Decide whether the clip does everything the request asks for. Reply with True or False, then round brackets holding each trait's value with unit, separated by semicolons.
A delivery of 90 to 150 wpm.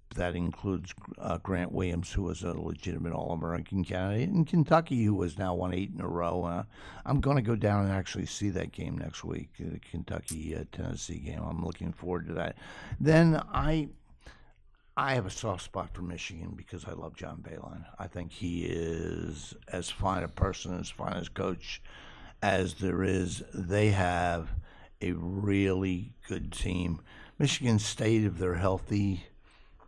False (165 wpm)